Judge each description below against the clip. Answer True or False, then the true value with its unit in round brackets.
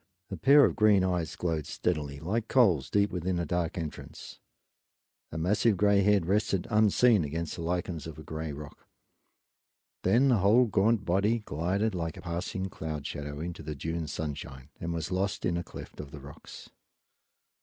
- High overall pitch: False (85 Hz)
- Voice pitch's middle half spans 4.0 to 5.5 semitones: True (4.4 semitones)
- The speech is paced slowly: False (175 wpm)